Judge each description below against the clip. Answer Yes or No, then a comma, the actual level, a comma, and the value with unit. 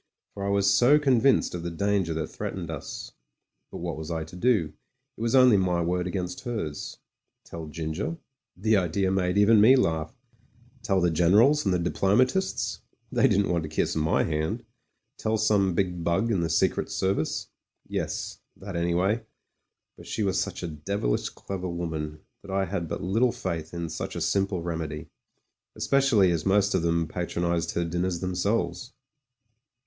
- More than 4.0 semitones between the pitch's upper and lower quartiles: No, average, 3.4 semitones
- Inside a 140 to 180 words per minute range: Yes, average, 170 wpm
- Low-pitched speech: Yes, very low, 90 Hz